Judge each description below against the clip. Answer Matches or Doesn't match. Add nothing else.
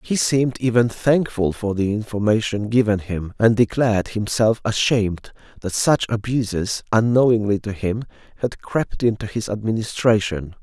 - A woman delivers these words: Doesn't match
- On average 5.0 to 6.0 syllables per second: Doesn't match